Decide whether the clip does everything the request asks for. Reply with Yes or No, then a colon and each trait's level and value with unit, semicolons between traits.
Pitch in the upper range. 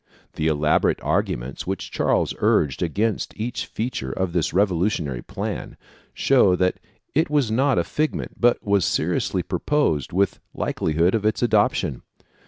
No: very low, 95 Hz